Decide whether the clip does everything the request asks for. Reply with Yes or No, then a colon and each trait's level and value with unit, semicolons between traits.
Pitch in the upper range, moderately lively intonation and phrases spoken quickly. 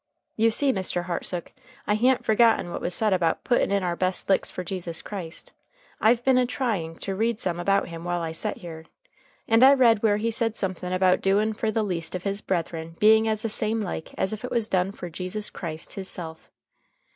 Yes: high, 195 Hz; average, 3.9 semitones; fast, 215 wpm